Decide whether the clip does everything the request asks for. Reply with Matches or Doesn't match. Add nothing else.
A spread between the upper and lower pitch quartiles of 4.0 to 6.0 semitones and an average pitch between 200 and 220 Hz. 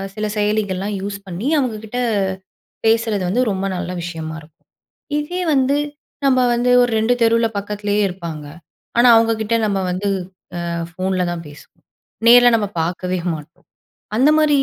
Matches